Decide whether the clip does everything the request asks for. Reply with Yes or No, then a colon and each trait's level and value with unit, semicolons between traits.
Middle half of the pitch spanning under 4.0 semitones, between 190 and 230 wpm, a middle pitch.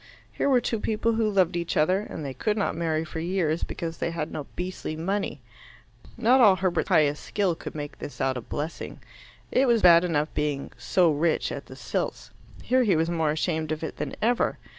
No: average, 4.5 semitones; fast, 205 wpm; medium, 170 Hz